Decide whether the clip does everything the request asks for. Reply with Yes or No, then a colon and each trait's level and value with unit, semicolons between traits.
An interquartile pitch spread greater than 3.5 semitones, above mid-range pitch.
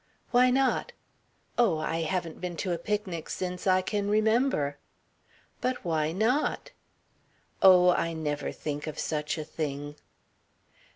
No: average, 5.2 semitones; medium, 180 Hz